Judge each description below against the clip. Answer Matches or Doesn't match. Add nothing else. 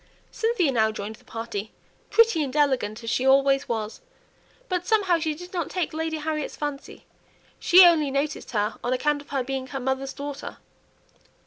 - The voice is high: Matches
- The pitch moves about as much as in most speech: Matches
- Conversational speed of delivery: Matches